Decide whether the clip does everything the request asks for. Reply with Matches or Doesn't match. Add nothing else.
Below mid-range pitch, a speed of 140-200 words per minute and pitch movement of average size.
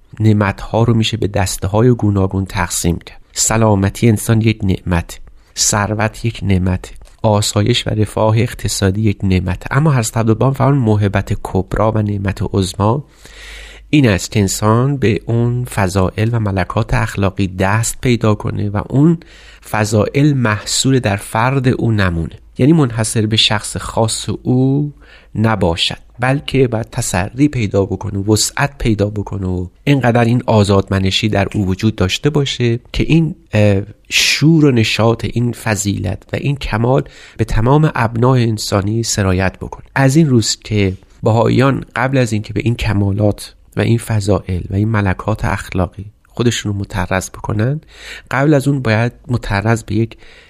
Matches